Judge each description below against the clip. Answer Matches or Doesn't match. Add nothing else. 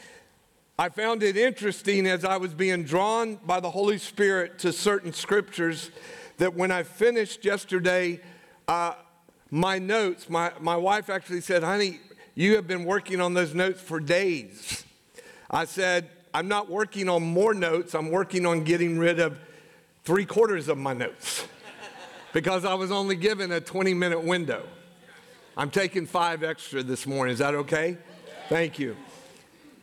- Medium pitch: Matches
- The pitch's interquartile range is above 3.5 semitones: Doesn't match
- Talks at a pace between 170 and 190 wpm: Doesn't match